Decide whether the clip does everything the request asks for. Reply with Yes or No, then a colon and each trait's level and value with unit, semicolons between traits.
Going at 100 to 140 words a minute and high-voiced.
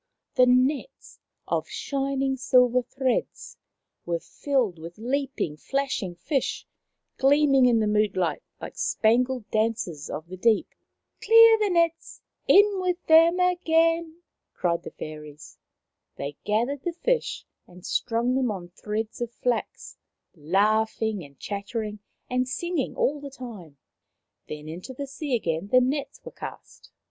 Yes: slow, 135 wpm; very high, 250 Hz